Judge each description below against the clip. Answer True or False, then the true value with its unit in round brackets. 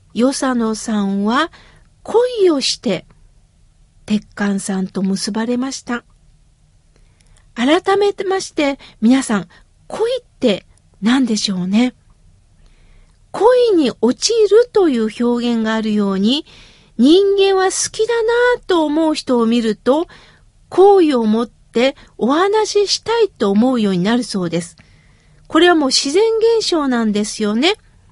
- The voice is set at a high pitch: True (260 Hz)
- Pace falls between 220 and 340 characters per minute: True (235 characters per minute)